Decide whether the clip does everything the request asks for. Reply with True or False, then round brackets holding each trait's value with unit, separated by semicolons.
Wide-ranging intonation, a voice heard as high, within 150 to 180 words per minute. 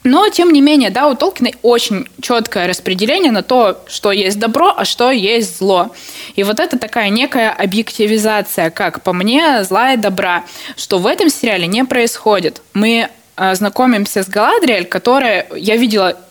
False (4.2 semitones; 220 Hz; 160 wpm)